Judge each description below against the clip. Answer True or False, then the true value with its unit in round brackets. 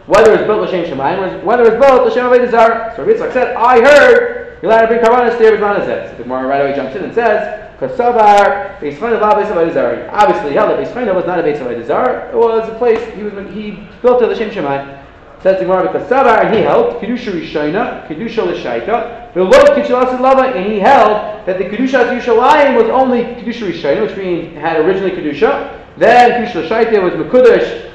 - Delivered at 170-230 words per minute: True (200 wpm)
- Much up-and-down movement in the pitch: False (3.8 semitones)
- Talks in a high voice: True (225 Hz)